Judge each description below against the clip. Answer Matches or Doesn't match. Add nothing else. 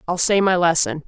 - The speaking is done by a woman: Matches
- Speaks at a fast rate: Matches